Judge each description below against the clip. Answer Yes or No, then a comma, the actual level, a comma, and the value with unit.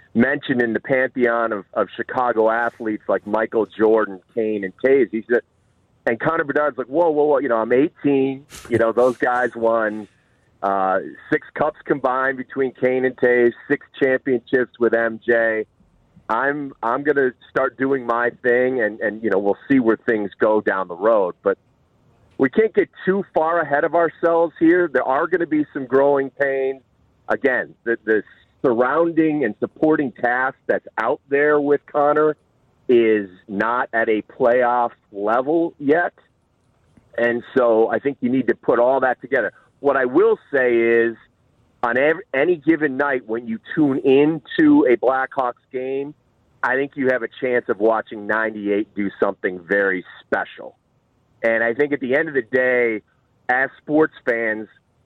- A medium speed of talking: Yes, average, 165 wpm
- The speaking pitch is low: Yes, low, 125 Hz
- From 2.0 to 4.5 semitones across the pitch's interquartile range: Yes, average, 4.2 semitones